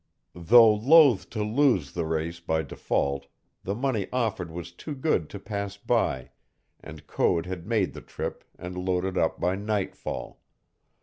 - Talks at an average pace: Yes, average, 150 wpm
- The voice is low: Yes, very low, 95 Hz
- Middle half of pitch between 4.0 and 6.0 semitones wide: Yes, average, 4.7 semitones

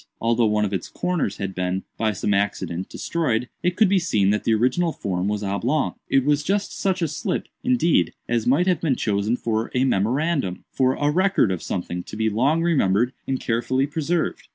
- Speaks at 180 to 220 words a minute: Yes, average, 195 wpm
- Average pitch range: No, wide, 7.7 semitones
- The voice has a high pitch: No, low, 125 Hz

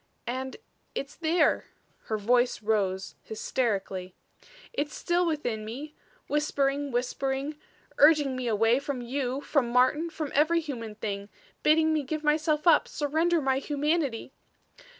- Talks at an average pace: No, slow, 130 wpm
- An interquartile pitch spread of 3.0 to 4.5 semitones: Yes, average, 4.2 semitones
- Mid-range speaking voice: No, very high, 275 Hz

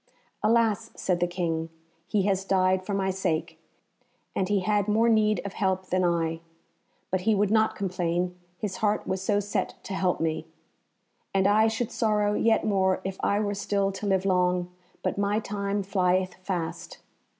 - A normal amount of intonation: No, narrow, 2.2 semitones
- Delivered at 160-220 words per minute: Yes, average, 170 wpm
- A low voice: No, high, 195 Hz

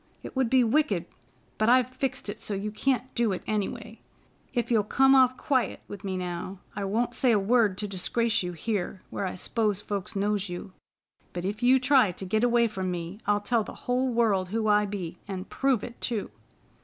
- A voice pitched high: Yes, high, 210 Hz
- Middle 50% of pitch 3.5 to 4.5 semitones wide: Yes, average, 3.9 semitones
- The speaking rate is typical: No, fast, 210 wpm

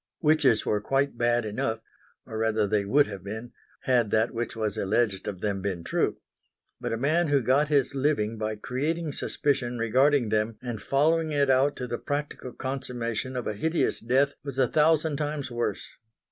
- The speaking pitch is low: Yes, low, 125 Hz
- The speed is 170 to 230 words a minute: Yes, average, 180 wpm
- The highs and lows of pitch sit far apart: No, average, 4.6 semitones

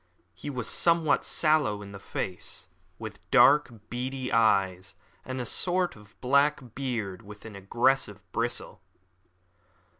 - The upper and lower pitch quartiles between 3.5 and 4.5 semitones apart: No, average, 5.2 semitones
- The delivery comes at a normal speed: No, slow, 120 wpm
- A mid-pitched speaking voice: No, low, 120 Hz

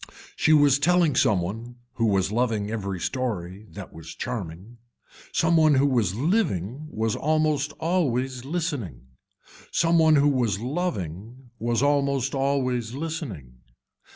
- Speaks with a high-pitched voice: No, low, 125 Hz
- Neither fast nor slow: No, slow, 130 wpm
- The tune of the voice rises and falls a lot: Yes, wide, 6.1 semitones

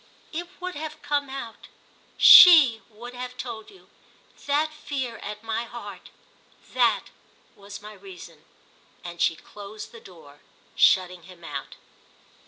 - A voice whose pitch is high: Yes, high, 225 Hz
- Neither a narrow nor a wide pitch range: No, wide, 7.1 semitones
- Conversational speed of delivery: No, slow, 120 wpm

